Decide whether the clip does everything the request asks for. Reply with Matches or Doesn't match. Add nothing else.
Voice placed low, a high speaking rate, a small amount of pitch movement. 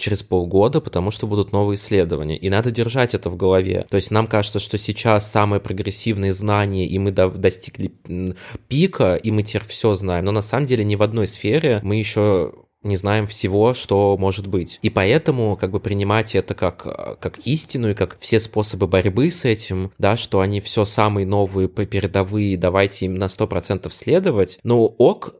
Matches